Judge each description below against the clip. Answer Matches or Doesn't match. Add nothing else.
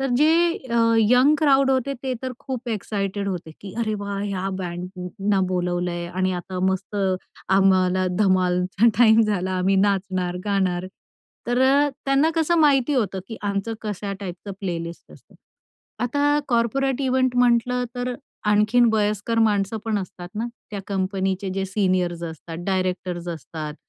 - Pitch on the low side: Doesn't match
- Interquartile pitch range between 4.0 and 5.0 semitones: Matches